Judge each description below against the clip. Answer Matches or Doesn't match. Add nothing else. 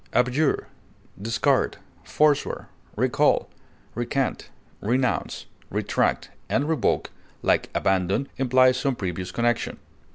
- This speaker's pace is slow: Matches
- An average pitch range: Matches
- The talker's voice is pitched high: Doesn't match